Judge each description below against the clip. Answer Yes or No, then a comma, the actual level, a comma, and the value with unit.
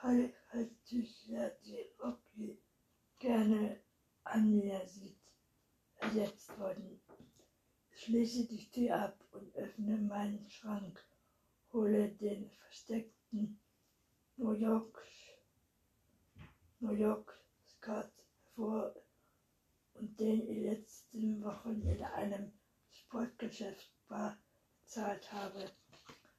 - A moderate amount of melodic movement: No, narrow, 1.9 semitones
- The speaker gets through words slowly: Yes, slow, 85 wpm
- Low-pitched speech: No, high, 215 Hz